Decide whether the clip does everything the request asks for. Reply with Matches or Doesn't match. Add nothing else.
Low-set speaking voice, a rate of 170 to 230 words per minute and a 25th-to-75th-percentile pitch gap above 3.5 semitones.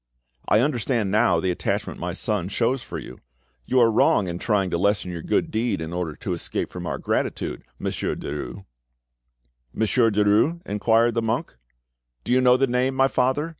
Matches